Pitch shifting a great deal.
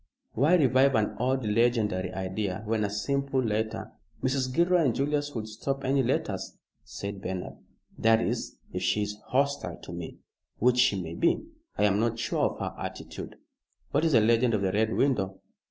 No: average, 4.5 semitones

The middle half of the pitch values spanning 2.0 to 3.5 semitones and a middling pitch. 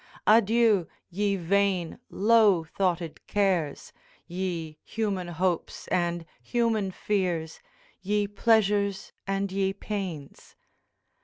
No: average, 3.0 semitones; high, 195 Hz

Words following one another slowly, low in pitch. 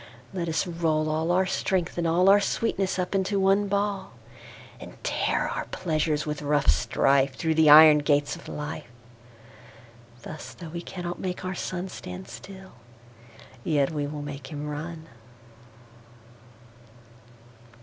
No: slow, 125 wpm; medium, 155 Hz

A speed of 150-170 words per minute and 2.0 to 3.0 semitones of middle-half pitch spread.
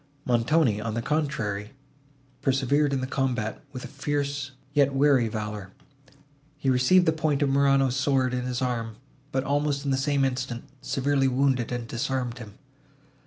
Yes: average, 160 wpm; narrow, 2.6 semitones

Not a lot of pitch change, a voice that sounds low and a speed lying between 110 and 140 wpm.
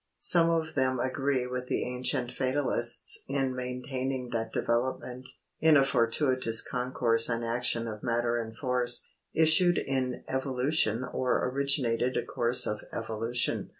Yes: narrow, 2.1 semitones; low, 125 Hz; slow, 135 wpm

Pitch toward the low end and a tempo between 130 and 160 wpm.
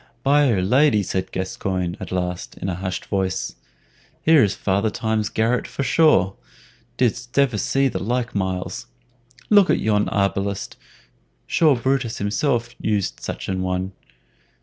Yes: low, 105 Hz; average, 145 wpm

